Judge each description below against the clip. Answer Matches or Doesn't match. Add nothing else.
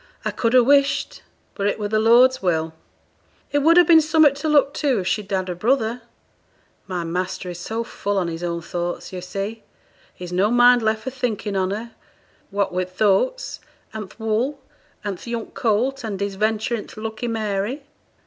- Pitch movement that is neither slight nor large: Matches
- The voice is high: Matches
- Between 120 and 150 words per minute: Doesn't match